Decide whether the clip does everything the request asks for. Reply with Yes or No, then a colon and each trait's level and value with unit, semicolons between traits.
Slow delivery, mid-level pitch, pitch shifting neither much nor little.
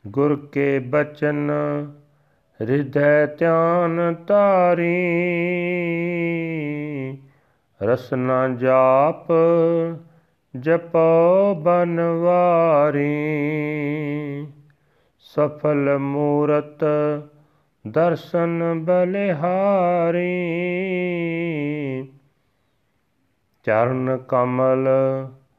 Yes: slow, 40 wpm; medium, 150 Hz; average, 3.1 semitones